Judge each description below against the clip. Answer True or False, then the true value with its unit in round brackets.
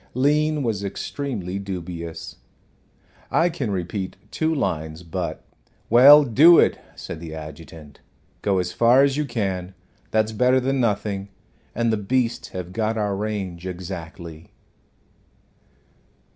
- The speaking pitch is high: False (100 Hz)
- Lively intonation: True (6.0 semitones)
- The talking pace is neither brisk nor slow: False (130 wpm)